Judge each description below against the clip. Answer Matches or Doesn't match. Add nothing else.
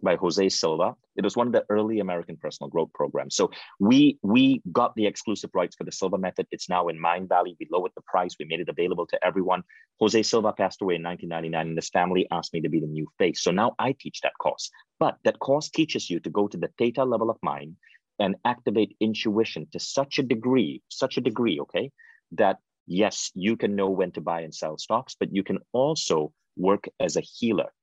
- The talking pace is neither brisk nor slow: Doesn't match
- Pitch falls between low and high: Doesn't match